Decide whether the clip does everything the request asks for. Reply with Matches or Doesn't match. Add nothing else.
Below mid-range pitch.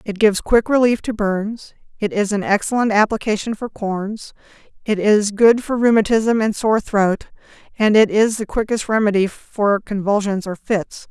Doesn't match